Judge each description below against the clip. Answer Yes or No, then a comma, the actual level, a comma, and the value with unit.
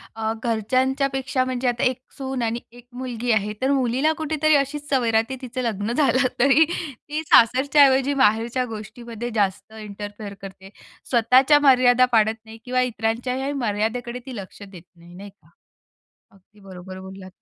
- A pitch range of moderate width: Yes, average, 3.7 semitones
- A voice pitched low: No, high, 240 Hz